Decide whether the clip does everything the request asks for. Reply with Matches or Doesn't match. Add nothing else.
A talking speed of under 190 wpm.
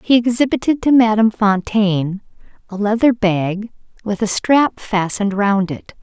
Matches